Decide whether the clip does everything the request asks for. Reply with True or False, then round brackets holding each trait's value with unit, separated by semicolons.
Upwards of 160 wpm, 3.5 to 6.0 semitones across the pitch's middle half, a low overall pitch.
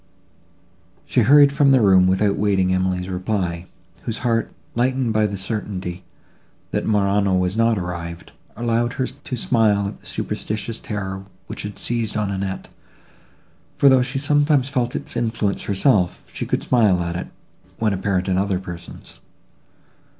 False (150 wpm; 4.1 semitones; 105 Hz)